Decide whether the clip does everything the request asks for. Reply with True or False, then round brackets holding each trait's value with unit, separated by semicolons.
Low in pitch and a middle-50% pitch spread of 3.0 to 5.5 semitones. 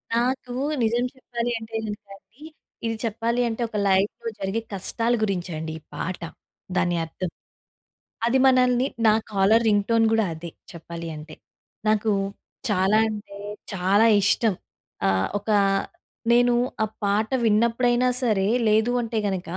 False (215 Hz; 3.4 semitones)